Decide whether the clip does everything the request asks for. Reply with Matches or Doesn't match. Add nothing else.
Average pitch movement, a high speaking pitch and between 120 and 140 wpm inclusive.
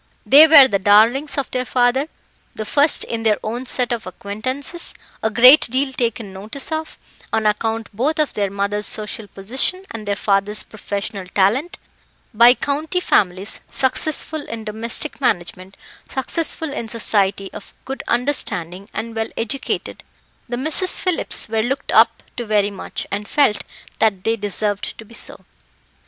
Doesn't match